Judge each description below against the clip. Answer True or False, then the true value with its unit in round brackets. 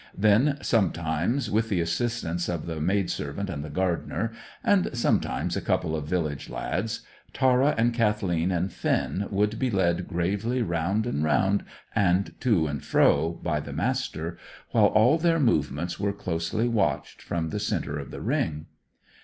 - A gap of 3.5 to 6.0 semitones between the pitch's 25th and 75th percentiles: True (5.6 semitones)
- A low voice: True (95 Hz)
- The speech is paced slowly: False (155 wpm)